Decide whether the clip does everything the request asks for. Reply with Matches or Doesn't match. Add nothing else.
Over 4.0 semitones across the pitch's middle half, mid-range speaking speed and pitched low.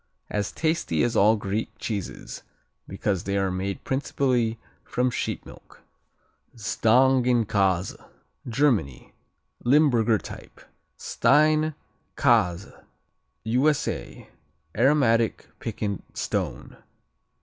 Doesn't match